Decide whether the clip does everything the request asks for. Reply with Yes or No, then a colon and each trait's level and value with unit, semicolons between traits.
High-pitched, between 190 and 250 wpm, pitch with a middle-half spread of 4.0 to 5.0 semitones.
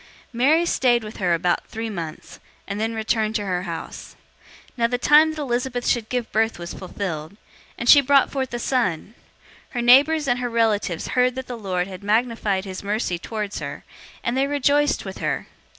Yes: high, 230 Hz; average, 200 wpm; average, 4.3 semitones